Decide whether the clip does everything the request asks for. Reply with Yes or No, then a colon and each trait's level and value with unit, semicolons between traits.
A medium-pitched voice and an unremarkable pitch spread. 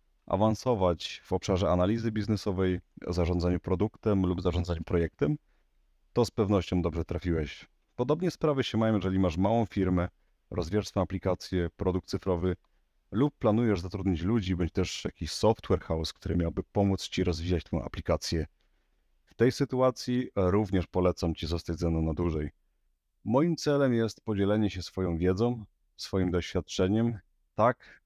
No: very low, 95 Hz; average, 4.0 semitones